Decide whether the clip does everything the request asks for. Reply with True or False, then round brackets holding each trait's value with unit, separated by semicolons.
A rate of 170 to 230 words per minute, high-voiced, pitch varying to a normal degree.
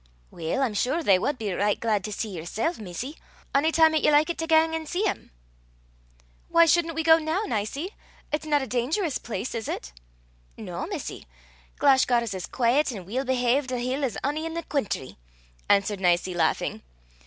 False (190 wpm; 260 Hz; 7.1 semitones)